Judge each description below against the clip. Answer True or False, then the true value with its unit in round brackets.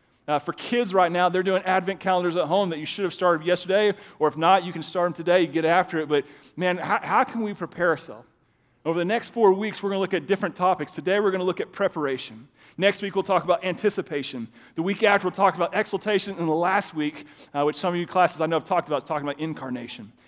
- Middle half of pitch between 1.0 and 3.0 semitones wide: False (3.8 semitones)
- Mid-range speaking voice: True (180 Hz)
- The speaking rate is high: True (260 wpm)